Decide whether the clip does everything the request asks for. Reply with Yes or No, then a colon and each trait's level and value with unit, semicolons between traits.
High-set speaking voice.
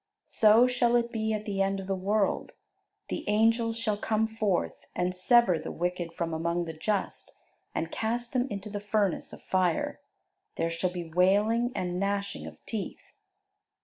Yes: high, 200 Hz